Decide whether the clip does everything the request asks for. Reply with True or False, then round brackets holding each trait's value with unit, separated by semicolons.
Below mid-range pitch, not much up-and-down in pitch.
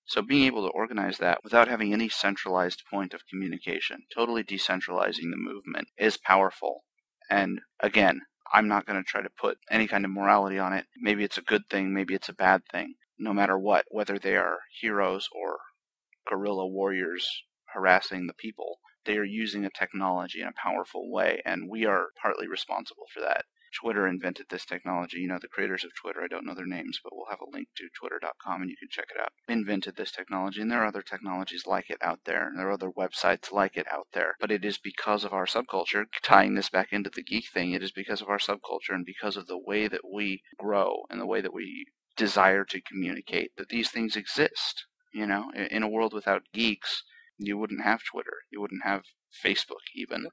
True (100 Hz; 2.1 semitones)